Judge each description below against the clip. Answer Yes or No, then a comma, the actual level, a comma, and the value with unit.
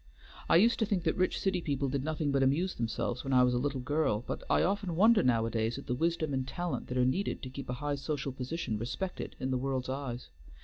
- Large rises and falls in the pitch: No, average, 4.8 semitones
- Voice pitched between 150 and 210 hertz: No, medium, 140 Hz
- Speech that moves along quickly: Yes, fast, 245 wpm